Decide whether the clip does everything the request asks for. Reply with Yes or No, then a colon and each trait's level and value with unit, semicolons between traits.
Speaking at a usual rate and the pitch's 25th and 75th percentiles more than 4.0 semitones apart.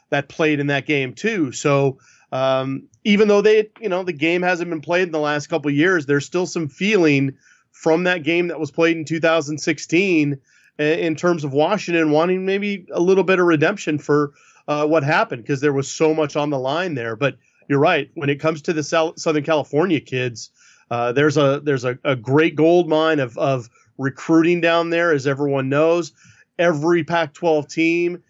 No: average, 195 wpm; average, 3.1 semitones